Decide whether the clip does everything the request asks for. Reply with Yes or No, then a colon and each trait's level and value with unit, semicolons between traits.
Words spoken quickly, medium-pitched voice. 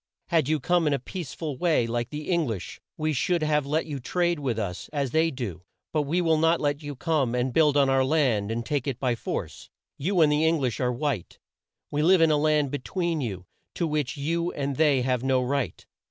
Yes: fast, 235 wpm; medium, 145 Hz